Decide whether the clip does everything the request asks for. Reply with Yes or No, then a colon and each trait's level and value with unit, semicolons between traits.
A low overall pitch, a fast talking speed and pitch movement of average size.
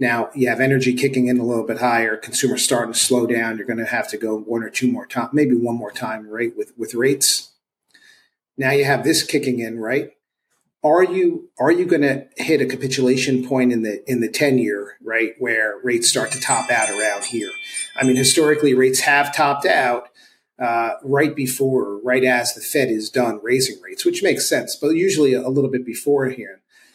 Yes: low, 130 Hz; fast, 210 wpm; average, 3.5 semitones